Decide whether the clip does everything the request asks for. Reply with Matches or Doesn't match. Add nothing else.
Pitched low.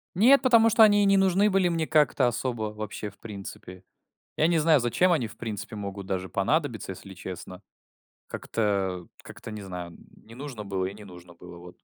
Matches